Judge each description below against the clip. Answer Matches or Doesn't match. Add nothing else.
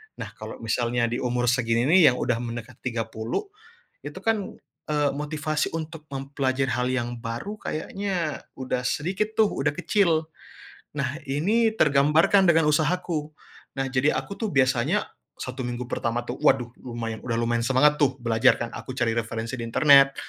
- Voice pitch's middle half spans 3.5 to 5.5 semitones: Matches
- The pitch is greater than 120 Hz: Matches